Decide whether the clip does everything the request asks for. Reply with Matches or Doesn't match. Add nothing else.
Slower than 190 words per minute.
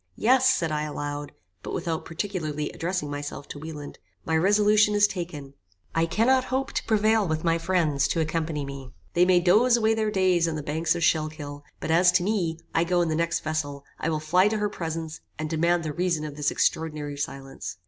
Doesn't match